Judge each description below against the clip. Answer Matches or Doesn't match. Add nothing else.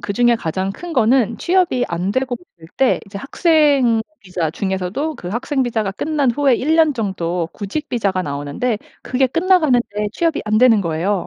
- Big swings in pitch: Matches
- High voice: Matches